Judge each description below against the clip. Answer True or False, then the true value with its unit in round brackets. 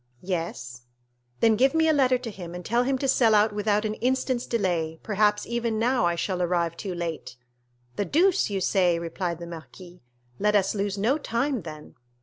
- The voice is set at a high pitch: True (205 Hz)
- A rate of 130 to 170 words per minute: False (190 wpm)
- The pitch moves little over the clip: False (5.4 semitones)